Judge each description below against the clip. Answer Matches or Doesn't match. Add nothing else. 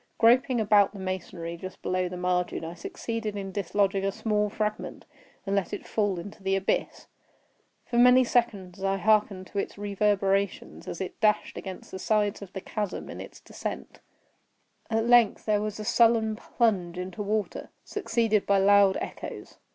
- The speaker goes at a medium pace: Matches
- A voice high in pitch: Matches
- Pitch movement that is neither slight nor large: Doesn't match